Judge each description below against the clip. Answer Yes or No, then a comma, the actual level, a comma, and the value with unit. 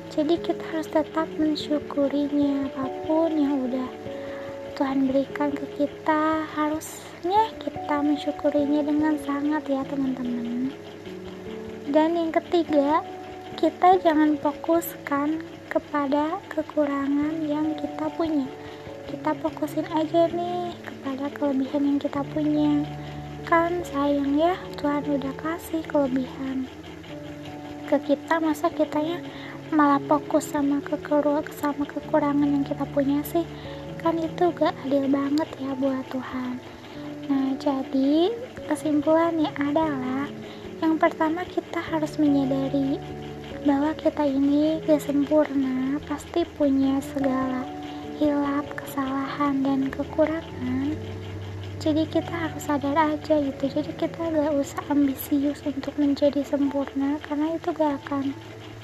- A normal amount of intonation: No, narrow, 2.2 semitones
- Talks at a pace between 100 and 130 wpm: Yes, average, 110 wpm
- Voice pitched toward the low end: No, very high, 290 Hz